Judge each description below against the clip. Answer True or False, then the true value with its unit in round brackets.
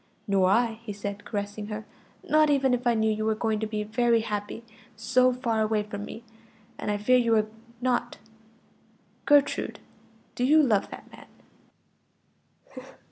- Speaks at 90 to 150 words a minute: False (160 wpm)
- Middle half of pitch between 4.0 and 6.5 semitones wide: False (3.0 semitones)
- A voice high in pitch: True (220 Hz)